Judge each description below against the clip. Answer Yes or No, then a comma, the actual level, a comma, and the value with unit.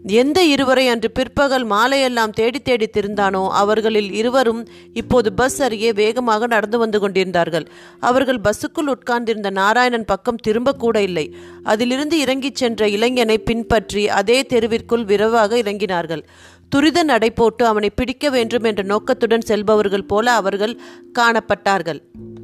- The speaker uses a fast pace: No, average, 120 wpm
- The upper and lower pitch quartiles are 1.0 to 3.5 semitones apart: Yes, average, 3.2 semitones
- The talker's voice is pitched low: No, high, 230 Hz